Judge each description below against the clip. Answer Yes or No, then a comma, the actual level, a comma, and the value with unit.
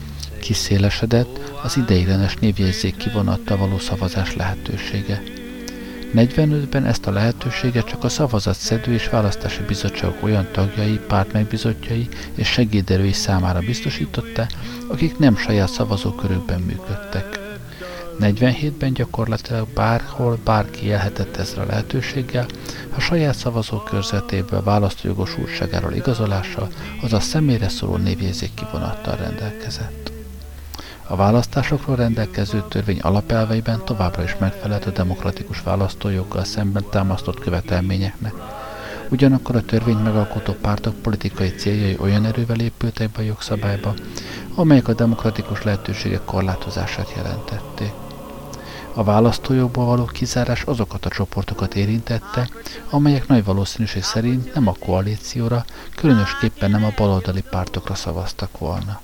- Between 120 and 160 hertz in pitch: No, low, 105 Hz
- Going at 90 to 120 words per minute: Yes, average, 110 wpm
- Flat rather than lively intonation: No, average, 3.3 semitones